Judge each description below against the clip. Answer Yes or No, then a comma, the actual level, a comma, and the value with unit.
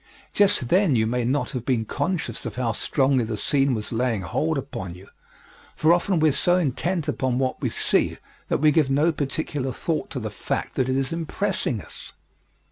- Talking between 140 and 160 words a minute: No, average, 200 wpm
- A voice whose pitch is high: No, low, 135 Hz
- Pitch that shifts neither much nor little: Yes, average, 4.7 semitones